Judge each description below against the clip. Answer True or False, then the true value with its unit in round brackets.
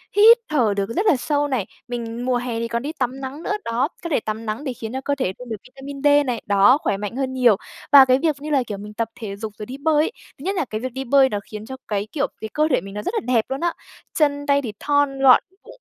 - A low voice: False (260 Hz)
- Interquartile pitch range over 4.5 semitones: False (4.2 semitones)